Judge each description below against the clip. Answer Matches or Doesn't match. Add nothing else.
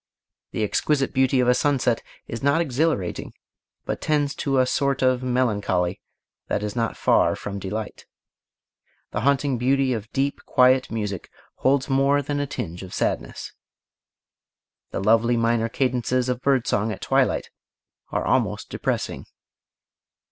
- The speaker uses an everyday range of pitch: Matches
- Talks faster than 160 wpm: Doesn't match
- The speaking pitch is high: Doesn't match